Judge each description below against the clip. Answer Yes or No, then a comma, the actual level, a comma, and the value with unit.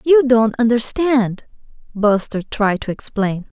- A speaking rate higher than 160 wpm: No, slow, 115 wpm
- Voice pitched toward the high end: Yes, high, 230 Hz